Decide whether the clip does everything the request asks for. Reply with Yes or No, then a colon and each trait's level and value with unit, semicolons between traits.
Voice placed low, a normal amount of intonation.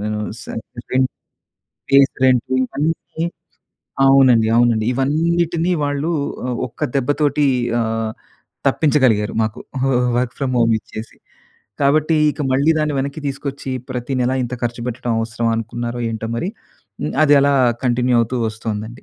Yes: low, 130 Hz; average, 3.6 semitones